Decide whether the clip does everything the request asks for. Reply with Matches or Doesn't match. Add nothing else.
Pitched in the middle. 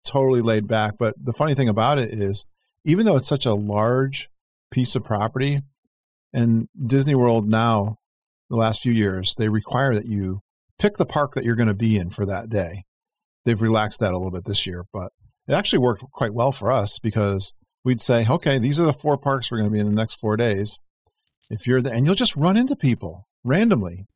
Doesn't match